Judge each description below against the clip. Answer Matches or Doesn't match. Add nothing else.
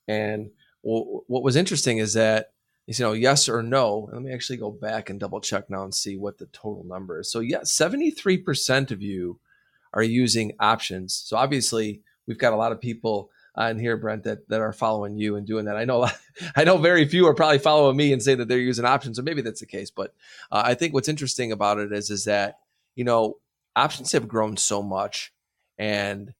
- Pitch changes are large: Doesn't match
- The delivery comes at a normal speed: Doesn't match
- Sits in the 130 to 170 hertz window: Doesn't match